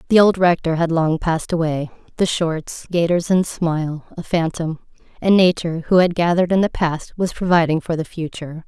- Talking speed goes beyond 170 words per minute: Yes, average, 180 wpm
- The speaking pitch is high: No, medium, 170 Hz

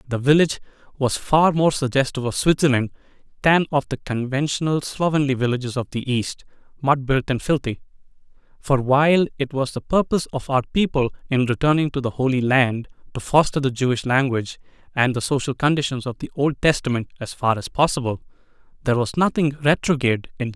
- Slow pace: No, average, 175 wpm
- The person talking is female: No, male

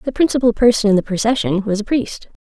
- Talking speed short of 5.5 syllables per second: No, 6.4 syllables/s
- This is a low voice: No, high, 225 Hz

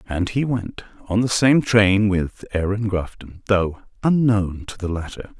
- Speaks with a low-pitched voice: Yes, low, 100 Hz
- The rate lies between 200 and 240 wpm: No, average, 165 wpm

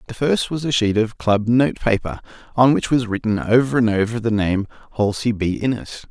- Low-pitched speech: Yes, low, 115 Hz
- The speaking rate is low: No, fast, 205 wpm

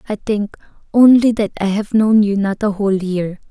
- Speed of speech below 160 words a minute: No, fast, 205 wpm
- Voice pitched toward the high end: Yes, high, 205 Hz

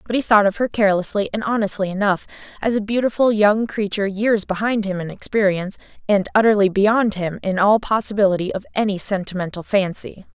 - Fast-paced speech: No, average, 175 wpm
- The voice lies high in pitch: Yes, high, 205 Hz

